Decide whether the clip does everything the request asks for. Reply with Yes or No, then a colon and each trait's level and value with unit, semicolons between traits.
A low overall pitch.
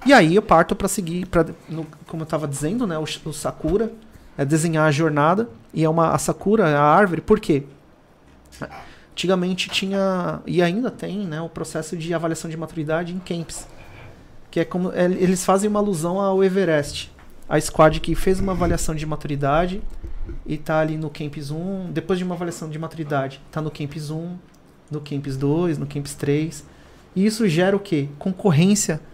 No: medium, 165 Hz